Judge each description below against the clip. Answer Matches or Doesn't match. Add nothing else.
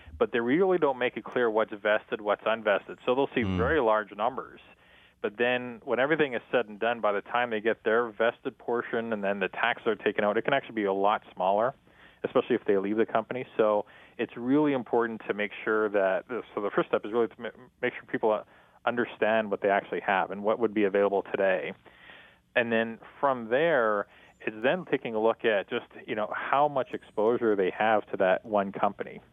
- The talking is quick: Matches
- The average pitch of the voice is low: Matches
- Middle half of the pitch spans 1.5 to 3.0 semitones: Matches